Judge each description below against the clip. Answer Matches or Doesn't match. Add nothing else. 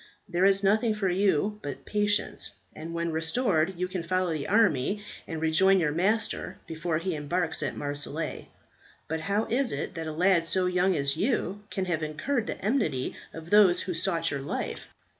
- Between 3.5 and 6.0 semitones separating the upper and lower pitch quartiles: Matches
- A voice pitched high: Doesn't match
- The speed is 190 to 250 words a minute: Doesn't match